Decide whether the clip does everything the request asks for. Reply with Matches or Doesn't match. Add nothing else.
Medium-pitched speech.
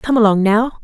Doesn't match